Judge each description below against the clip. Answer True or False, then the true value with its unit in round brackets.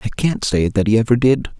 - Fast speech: True (265 wpm)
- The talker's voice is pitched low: True (115 Hz)